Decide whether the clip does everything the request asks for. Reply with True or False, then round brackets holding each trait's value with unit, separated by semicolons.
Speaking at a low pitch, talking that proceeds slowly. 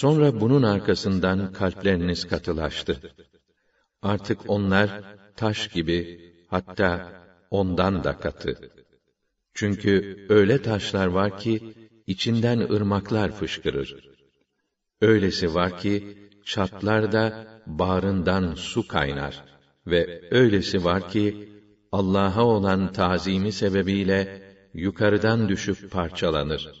True (100 Hz; 85 wpm)